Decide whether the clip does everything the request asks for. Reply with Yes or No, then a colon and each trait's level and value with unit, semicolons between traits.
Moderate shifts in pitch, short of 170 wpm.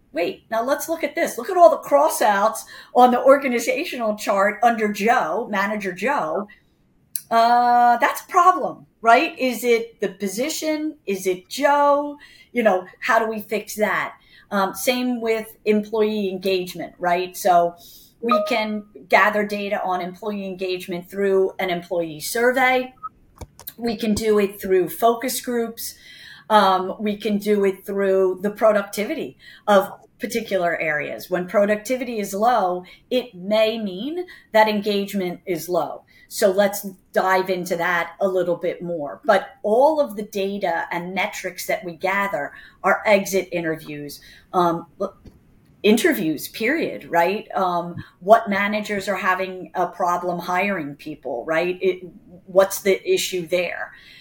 Yes: average, 4.0 semitones; average, 140 wpm